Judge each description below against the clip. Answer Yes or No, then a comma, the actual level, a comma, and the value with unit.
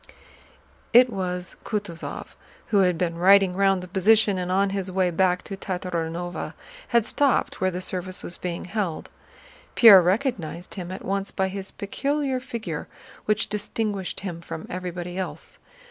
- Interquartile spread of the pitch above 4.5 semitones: No, narrow, 2.4 semitones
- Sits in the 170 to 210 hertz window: Yes, high, 190 Hz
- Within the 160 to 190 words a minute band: No, average, 150 wpm